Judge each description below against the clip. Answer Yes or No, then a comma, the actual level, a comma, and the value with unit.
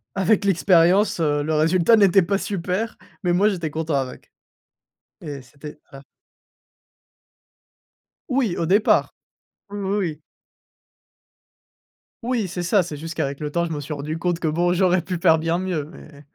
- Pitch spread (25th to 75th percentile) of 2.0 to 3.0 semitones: No, average, 3.7 semitones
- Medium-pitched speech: Yes, medium, 170 Hz